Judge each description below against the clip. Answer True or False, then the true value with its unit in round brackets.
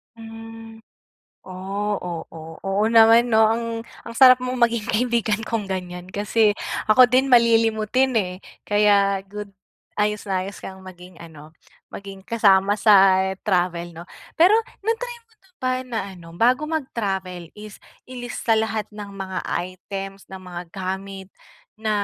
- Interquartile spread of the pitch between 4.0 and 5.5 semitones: False (3.3 semitones)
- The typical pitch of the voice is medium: False (210 Hz)